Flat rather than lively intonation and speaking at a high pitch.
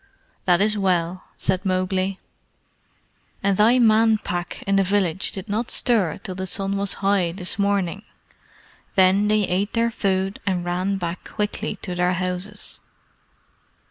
Yes: narrow, 1.9 semitones; high, 195 Hz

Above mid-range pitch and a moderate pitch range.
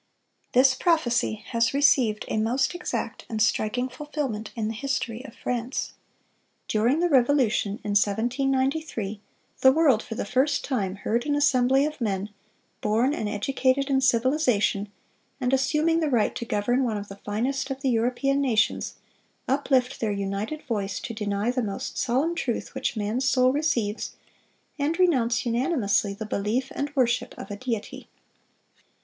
Yes: high, 245 Hz; average, 4.1 semitones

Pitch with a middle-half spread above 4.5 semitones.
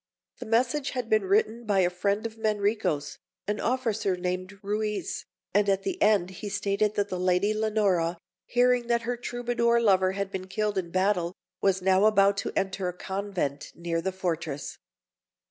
No: average, 2.8 semitones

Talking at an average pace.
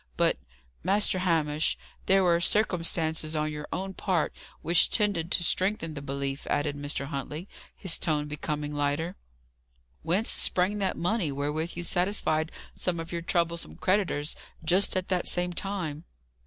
Yes: average, 145 wpm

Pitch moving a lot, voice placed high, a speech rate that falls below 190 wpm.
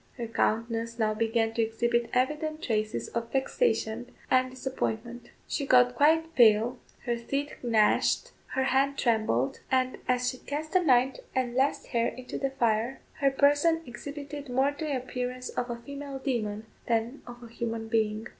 No: average, 3.1 semitones; very high, 250 Hz; average, 160 wpm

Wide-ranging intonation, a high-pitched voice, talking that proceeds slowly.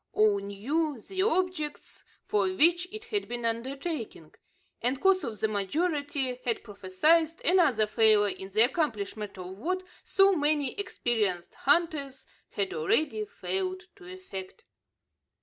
Yes: wide, 8.8 semitones; very high, 275 Hz; slow, 125 wpm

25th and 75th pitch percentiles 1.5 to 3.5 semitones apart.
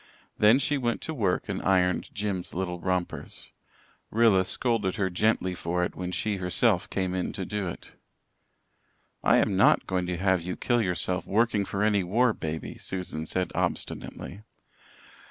Yes: average, 2.8 semitones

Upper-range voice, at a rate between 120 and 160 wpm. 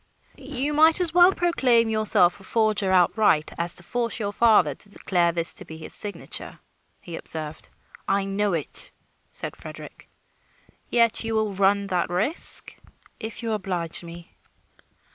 Yes: high, 205 Hz; average, 150 wpm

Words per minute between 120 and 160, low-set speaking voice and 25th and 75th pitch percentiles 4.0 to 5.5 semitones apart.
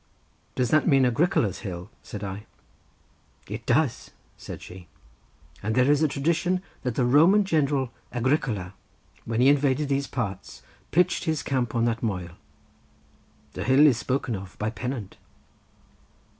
Yes: average, 145 wpm; low, 125 Hz; average, 5.0 semitones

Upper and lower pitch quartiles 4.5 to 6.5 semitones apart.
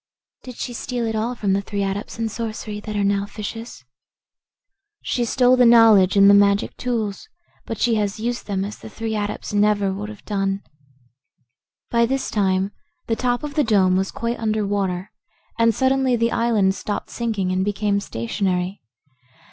No: average, 2.7 semitones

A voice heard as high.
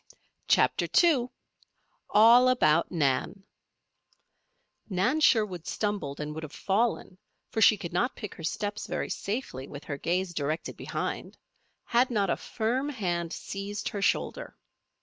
Yes: high, 200 Hz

